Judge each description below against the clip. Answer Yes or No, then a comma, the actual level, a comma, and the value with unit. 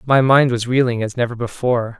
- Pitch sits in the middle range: No, low, 120 Hz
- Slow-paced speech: No, fast, 210 wpm